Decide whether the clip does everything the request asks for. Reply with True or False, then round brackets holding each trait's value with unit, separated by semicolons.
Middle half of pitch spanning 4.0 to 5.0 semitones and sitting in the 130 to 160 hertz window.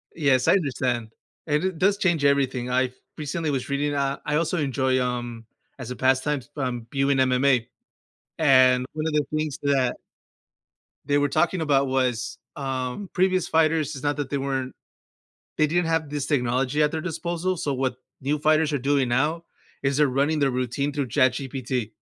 False (2.9 semitones; 140 Hz)